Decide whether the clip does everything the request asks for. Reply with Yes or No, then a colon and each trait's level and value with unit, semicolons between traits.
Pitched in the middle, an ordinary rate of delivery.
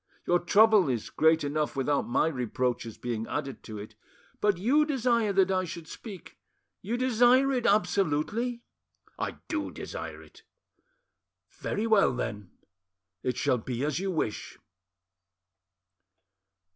No: medium, 175 Hz; slow, 130 wpm